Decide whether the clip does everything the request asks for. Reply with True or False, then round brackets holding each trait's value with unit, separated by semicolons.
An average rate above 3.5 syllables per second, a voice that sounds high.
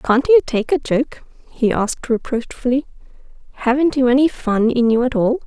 True (5.0 syllables/s; 245 Hz)